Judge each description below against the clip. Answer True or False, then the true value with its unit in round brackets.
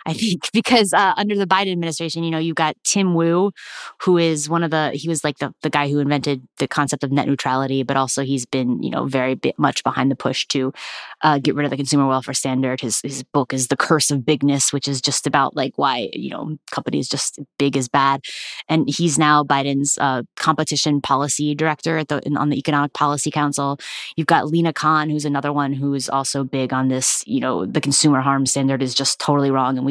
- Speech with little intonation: True (2.2 semitones)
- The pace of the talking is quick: True (230 wpm)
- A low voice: False (145 Hz)